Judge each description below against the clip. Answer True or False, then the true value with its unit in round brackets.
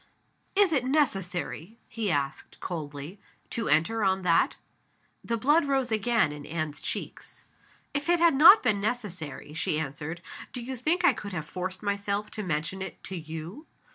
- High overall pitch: True (200 Hz)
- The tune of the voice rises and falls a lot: True (7.4 semitones)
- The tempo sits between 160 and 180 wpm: True (165 wpm)